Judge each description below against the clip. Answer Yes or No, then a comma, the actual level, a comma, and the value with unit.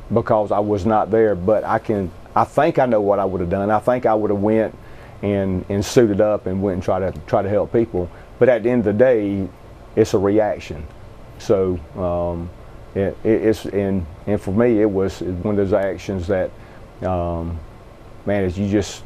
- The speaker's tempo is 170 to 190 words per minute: No, fast, 205 wpm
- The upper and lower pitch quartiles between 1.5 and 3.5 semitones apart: Yes, average, 2.8 semitones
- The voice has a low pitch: Yes, low, 100 Hz